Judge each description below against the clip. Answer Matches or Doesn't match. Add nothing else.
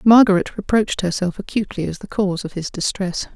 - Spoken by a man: Doesn't match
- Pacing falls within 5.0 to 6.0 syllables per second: Doesn't match